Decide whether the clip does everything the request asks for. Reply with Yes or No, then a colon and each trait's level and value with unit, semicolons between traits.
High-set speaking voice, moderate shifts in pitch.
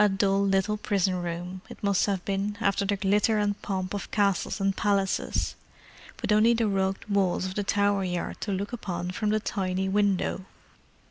No: high, 195 Hz; narrow, 1.4 semitones